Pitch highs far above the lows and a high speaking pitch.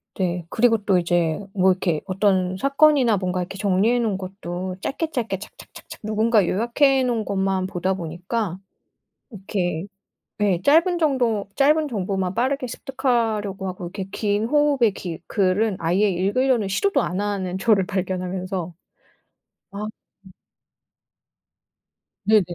No: average, 4.0 semitones; high, 200 Hz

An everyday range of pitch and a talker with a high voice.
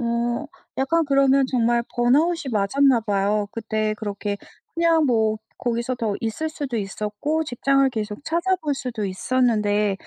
Yes: average, 4.5 semitones; high, 240 Hz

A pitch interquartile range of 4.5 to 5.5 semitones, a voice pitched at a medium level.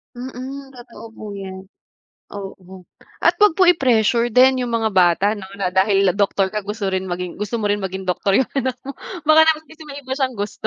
No: average, 5.2 semitones; high, 215 Hz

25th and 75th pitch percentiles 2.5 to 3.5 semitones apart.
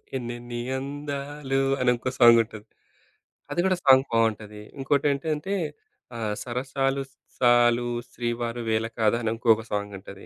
Yes: average, 3.1 semitones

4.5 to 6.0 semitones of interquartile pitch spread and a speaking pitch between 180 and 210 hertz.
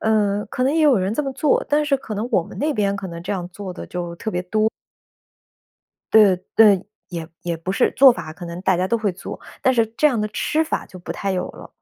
Yes: average, 5.1 semitones; high, 205 Hz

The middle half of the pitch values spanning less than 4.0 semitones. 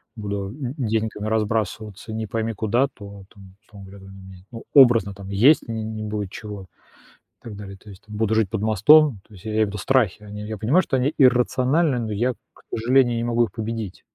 Yes: average, 2.7 semitones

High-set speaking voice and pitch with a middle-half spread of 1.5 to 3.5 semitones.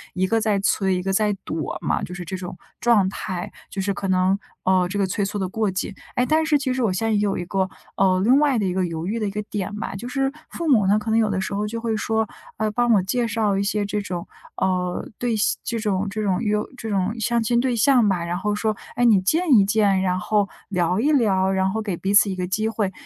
Yes: high, 205 Hz; average, 3.0 semitones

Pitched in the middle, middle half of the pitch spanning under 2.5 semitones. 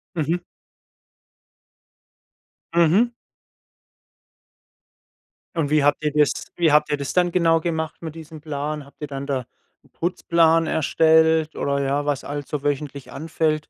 Yes: medium, 155 Hz; narrow, 2.1 semitones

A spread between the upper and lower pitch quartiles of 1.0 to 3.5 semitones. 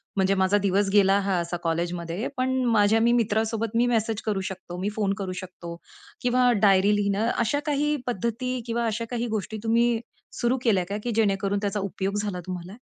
Yes: average, 3.2 semitones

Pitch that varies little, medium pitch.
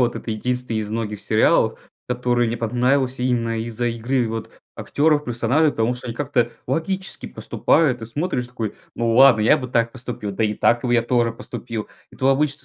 No: narrow, 2.3 semitones; low, 120 Hz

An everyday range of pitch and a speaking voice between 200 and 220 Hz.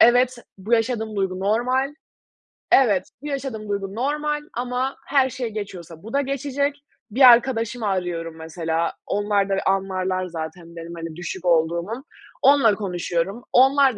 No: wide, 6.1 semitones; high, 210 Hz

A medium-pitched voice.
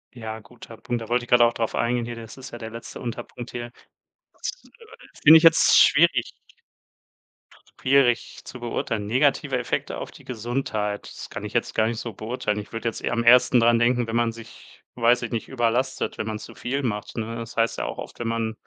No: low, 120 Hz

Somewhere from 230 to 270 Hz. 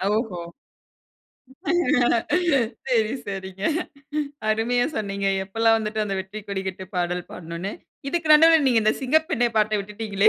No: high, 215 Hz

